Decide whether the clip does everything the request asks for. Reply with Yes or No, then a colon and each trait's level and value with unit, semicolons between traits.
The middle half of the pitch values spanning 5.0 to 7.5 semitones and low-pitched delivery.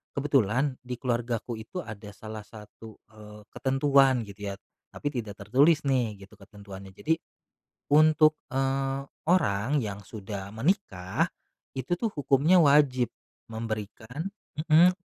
Yes: wide, 5.4 semitones; low, 125 Hz